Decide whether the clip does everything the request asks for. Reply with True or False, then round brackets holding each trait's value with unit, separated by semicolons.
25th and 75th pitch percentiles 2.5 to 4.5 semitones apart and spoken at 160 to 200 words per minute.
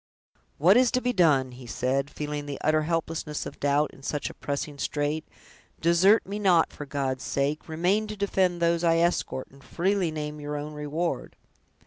True (3.3 semitones; 180 wpm)